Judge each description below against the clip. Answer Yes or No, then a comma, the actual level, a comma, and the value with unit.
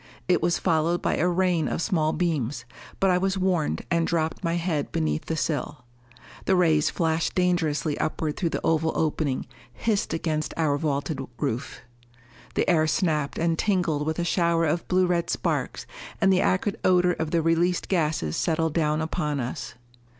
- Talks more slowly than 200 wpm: Yes, average, 170 wpm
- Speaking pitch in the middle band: Yes, medium, 165 Hz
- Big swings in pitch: No, narrow, 2.5 semitones